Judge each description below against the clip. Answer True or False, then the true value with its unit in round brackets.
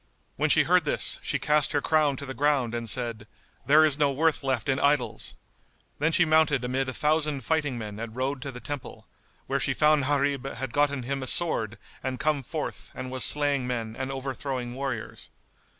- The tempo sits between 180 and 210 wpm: True (200 wpm)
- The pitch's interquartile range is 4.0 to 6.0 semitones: False (2.8 semitones)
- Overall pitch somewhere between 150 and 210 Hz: False (135 Hz)